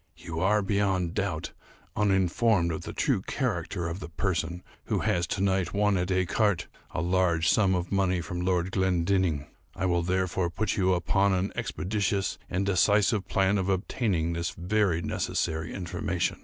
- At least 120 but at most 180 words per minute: Yes, average, 160 wpm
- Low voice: Yes, very low, 95 Hz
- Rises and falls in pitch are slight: Yes, narrow, 2.2 semitones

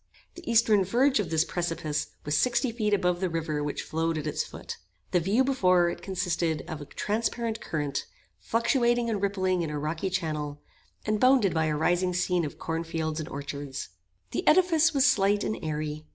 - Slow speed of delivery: No, average, 180 wpm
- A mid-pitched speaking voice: Yes, medium, 180 Hz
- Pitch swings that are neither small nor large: No, wide, 5.7 semitones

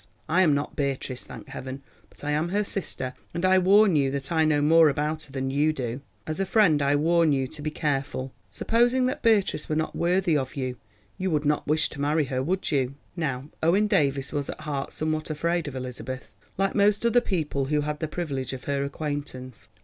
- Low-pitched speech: No, medium, 150 Hz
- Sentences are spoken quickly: Yes, fast, 215 wpm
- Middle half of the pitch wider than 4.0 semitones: No, average, 3.7 semitones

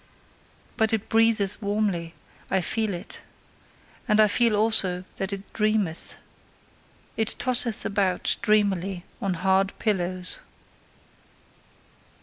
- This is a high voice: Yes, high, 200 Hz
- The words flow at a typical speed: No, slow, 105 wpm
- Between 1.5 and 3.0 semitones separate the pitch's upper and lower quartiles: Yes, average, 2.7 semitones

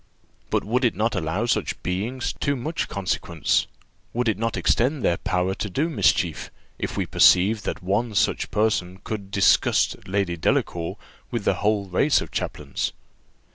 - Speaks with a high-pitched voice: No, low, 105 Hz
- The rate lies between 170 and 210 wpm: No, average, 160 wpm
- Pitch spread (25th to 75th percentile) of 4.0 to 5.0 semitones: Yes, average, 4.3 semitones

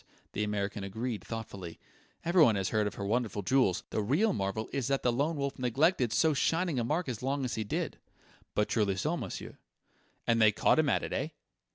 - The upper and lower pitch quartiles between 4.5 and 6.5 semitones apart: Yes, average, 5.1 semitones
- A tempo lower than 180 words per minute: No, fast, 205 wpm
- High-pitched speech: No, low, 120 Hz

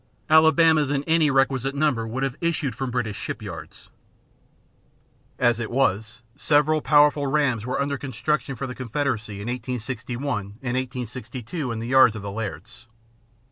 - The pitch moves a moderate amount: Yes, average, 3.8 semitones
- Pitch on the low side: Yes, low, 130 Hz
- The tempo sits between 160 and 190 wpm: No, average, 145 wpm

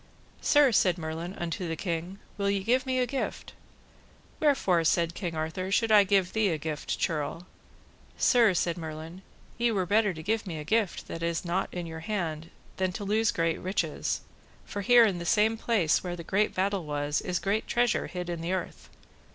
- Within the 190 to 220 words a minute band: Yes, average, 195 wpm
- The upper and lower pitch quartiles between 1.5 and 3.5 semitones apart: No, average, 4.2 semitones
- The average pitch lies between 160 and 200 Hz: Yes, medium, 185 Hz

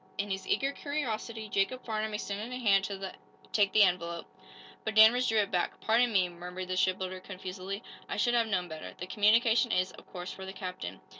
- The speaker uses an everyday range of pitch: Yes, average, 3.2 semitones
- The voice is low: No, high, 200 Hz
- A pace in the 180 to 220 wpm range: Yes, average, 200 wpm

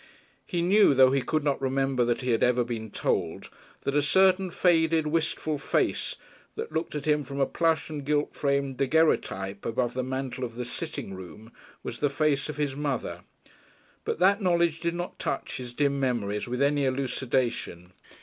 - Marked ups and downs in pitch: No, average, 3.8 semitones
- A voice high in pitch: No, medium, 140 Hz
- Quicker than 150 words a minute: Yes, average, 180 wpm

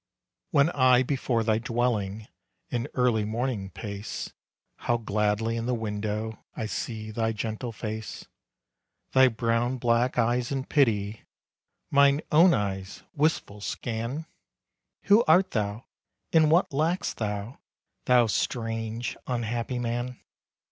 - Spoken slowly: Yes, slow, 120 wpm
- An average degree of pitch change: Yes, average, 3.0 semitones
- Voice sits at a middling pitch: No, low, 115 Hz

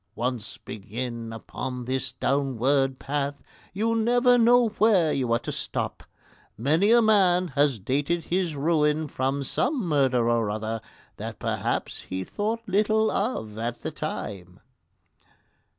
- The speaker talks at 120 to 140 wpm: Yes, slow, 135 wpm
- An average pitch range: No, wide, 8.5 semitones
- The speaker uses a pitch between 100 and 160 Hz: Yes, medium, 140 Hz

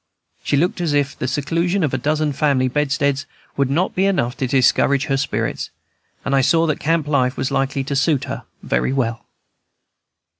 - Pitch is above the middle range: No, medium, 140 Hz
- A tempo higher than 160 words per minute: Yes, average, 185 wpm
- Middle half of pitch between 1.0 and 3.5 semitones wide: Yes, narrow, 2.4 semitones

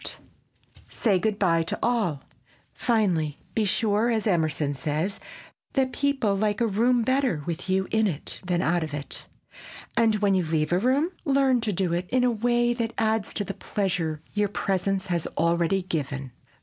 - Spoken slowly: No, average, 175 wpm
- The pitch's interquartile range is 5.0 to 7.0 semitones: Yes, average, 5.3 semitones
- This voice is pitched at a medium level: No, high, 195 Hz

